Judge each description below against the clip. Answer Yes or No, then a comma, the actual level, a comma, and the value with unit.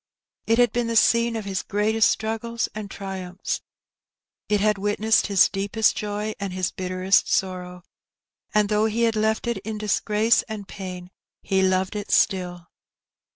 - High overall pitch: Yes, high, 210 Hz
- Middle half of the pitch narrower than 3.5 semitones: Yes, narrow, 2.5 semitones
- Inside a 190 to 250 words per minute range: No, average, 155 wpm